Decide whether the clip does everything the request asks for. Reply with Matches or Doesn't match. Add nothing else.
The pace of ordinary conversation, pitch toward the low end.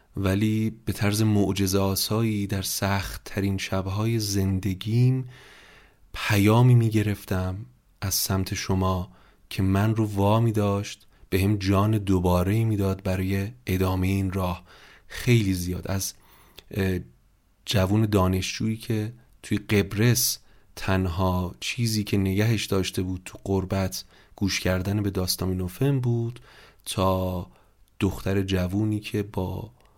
Matches